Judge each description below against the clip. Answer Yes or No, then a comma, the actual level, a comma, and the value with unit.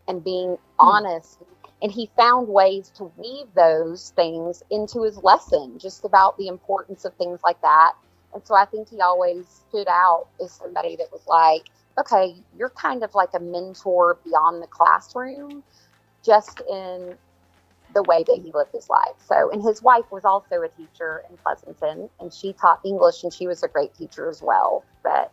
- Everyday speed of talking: Yes, average, 180 wpm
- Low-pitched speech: No, high, 190 Hz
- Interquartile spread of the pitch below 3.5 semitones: No, average, 3.8 semitones